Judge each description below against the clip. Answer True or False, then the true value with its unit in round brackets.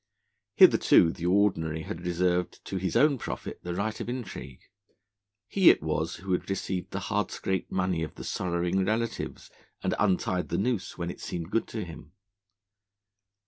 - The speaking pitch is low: True (90 Hz)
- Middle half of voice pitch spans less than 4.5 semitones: True (2.8 semitones)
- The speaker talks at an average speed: True (165 wpm)